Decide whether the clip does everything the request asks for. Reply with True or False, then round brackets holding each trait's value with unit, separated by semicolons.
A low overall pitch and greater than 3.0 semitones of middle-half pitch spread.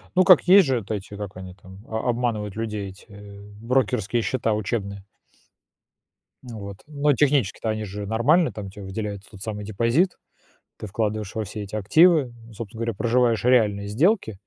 True (110 Hz; 3.5 semitones)